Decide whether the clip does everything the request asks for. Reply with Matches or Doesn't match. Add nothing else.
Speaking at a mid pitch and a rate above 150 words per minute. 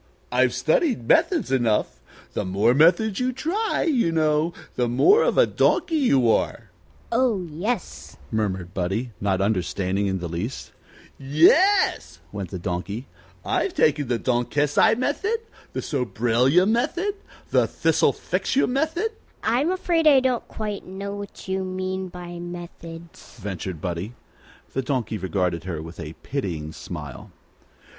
Doesn't match